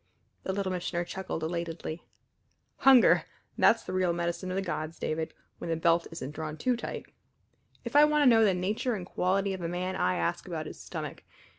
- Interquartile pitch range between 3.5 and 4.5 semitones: No, average, 3.0 semitones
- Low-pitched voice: No, medium, 180 Hz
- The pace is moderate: Yes, average, 195 wpm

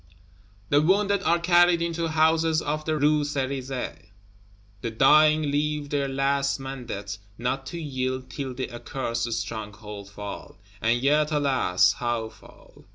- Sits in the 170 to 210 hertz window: No, low, 135 Hz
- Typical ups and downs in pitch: Yes, average, 4.3 semitones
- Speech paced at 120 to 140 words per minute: Yes, slow, 135 wpm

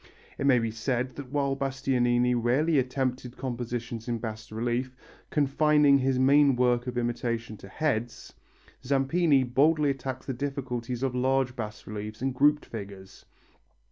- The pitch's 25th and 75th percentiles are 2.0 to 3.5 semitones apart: Yes, narrow, 2.4 semitones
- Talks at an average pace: Yes, average, 145 wpm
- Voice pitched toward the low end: Yes, low, 125 Hz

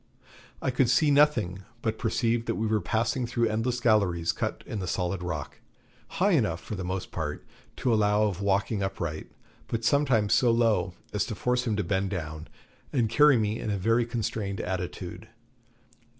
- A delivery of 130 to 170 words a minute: No, average, 180 wpm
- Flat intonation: No, average, 3.9 semitones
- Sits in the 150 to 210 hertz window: No, low, 110 Hz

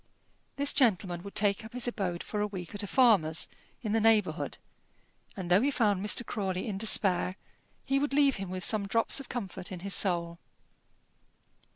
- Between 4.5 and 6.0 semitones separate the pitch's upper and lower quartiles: No, average, 3.6 semitones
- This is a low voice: No, high, 205 Hz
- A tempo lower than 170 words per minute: No, average, 185 wpm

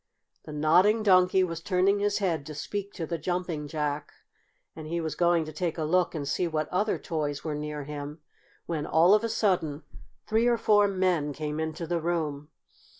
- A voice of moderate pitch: Yes, medium, 165 Hz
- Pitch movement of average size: Yes, average, 3.5 semitones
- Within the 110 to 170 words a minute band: No, average, 195 wpm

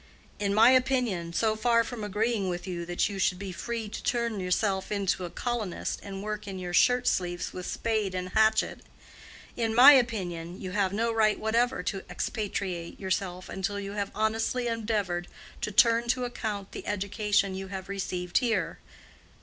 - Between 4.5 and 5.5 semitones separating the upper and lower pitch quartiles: No, average, 3.4 semitones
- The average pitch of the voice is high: Yes, high, 205 Hz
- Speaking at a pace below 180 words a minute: Yes, average, 170 wpm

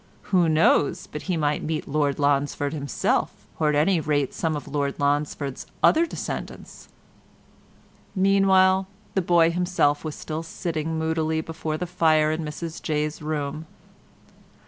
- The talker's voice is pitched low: No, medium, 155 Hz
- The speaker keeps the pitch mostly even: Yes, narrow, 2.2 semitones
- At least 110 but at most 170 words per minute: Yes, average, 140 wpm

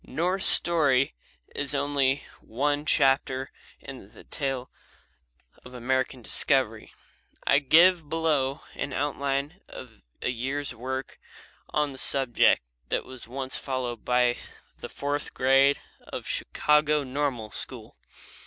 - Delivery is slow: Yes, slow, 120 wpm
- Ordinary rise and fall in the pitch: No, narrow, 2.0 semitones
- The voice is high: No, low, 135 Hz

